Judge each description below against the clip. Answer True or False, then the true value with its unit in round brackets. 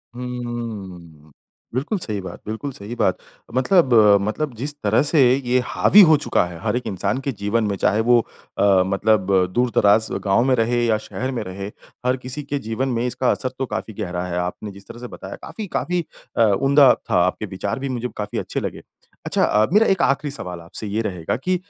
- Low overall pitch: True (115 Hz)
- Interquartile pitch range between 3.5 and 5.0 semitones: True (4.5 semitones)